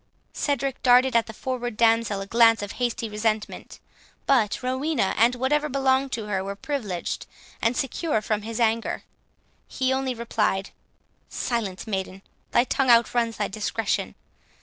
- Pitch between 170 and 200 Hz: No, high, 230 Hz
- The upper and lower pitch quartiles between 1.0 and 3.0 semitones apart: No, average, 3.5 semitones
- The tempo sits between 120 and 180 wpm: Yes, average, 145 wpm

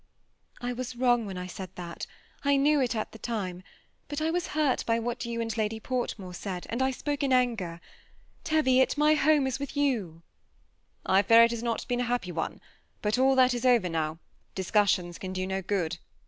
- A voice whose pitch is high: Yes, high, 235 Hz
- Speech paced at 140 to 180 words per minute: No, fast, 205 wpm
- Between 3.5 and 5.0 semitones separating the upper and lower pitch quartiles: No, wide, 5.5 semitones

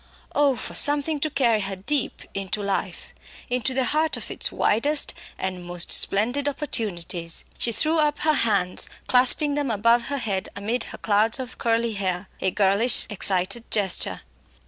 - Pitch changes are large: Yes, wide, 6.2 semitones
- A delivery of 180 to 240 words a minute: No, average, 160 wpm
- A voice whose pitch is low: No, high, 230 Hz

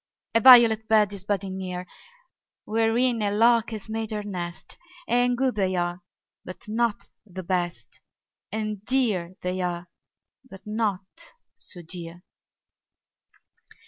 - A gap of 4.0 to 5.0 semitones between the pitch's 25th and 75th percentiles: No, average, 3.6 semitones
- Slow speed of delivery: Yes, slow, 125 wpm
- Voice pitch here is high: Yes, high, 205 Hz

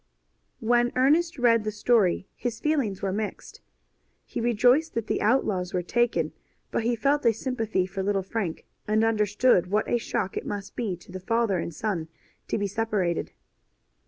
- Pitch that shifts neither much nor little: Yes, average, 3.8 semitones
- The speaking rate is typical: Yes, average, 170 wpm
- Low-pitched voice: No, high, 215 Hz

